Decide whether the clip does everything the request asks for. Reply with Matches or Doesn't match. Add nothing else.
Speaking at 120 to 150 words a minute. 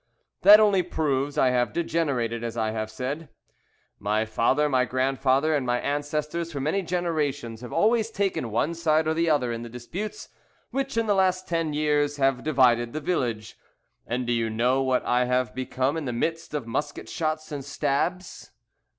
Doesn't match